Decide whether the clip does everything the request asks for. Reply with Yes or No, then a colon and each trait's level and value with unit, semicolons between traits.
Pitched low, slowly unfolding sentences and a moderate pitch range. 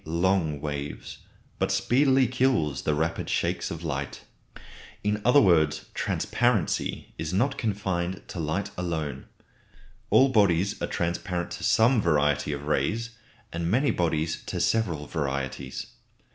No: very low, 85 Hz; slow, 130 wpm; wide, 5.9 semitones